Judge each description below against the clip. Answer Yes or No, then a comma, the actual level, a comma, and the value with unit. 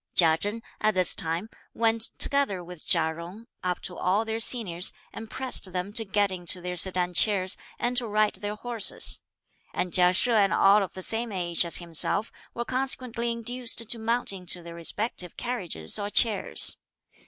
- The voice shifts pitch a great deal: No, average, 4.2 semitones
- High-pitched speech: Yes, high, 200 Hz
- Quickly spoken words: No, average, 175 wpm